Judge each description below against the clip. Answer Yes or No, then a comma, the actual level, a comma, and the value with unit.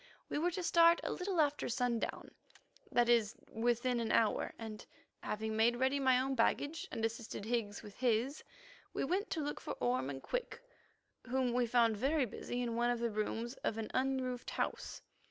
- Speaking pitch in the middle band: No, high, 240 Hz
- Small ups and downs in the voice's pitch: No, average, 3.2 semitones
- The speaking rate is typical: Yes, average, 185 wpm